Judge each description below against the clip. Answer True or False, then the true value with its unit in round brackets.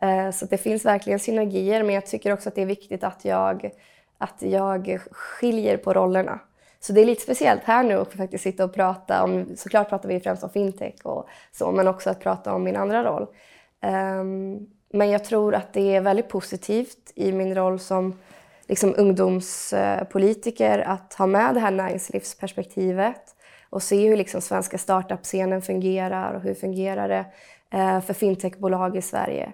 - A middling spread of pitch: False (1.5 semitones)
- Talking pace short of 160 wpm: False (170 wpm)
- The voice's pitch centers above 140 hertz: True (190 Hz)